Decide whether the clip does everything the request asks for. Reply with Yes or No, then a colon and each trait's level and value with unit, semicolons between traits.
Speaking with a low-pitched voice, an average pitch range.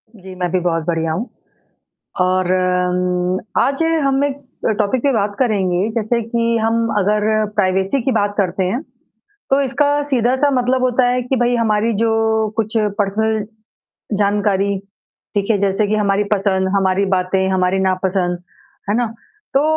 No: high, 205 Hz; average, 4.0 semitones